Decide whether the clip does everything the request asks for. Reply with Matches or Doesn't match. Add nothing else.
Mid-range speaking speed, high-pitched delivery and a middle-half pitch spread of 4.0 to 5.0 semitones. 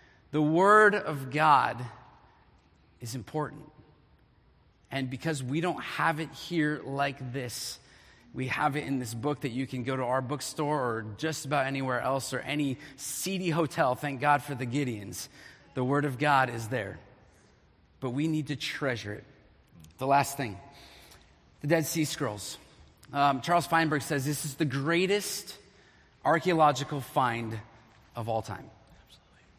Doesn't match